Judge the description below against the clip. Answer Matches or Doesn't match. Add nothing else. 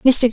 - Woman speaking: Matches